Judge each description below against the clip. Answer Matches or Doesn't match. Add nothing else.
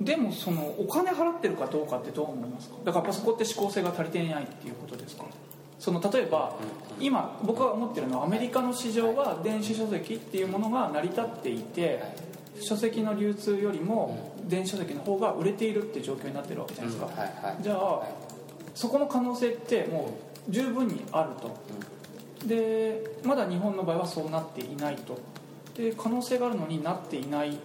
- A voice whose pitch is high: Matches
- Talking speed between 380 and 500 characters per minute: Matches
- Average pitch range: Doesn't match